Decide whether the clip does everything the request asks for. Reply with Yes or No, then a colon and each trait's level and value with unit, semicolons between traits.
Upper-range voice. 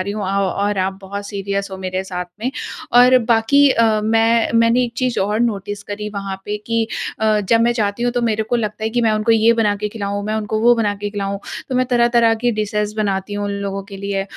Yes: high, 215 Hz